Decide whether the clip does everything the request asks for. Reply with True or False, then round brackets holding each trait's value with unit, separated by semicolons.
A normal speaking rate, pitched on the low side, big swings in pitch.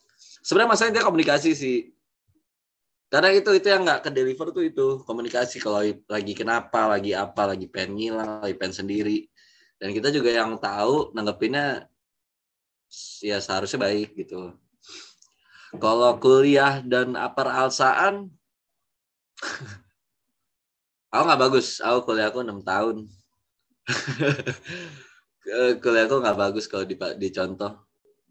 True (115 wpm; 120 Hz; 6.7 semitones)